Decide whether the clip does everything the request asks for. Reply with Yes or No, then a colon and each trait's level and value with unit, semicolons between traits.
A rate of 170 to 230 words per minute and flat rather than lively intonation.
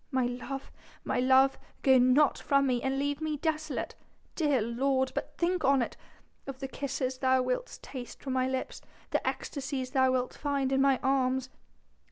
Yes: average, 175 wpm; narrow, 1.4 semitones